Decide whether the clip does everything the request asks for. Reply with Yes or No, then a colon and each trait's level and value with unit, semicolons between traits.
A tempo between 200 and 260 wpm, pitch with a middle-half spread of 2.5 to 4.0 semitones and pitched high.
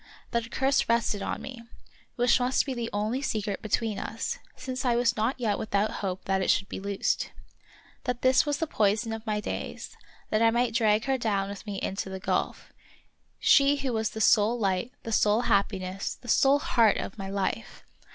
Yes: fast, 205 wpm; average, 3.5 semitones; high, 225 Hz